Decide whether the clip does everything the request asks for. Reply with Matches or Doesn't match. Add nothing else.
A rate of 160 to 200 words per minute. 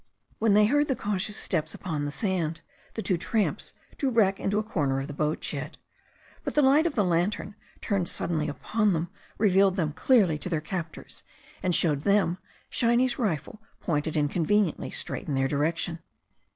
Matches